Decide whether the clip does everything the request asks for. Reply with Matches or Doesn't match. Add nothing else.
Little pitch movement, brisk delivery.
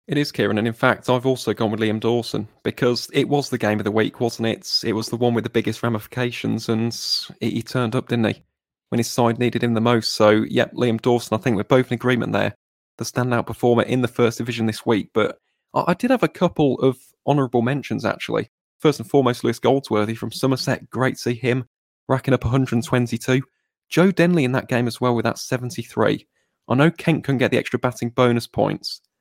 Matches